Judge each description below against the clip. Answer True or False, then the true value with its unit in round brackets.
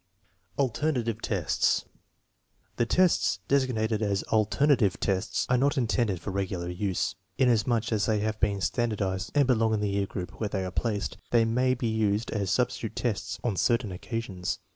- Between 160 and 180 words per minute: True (170 wpm)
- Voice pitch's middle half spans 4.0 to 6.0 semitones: False (3.5 semitones)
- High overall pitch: False (110 Hz)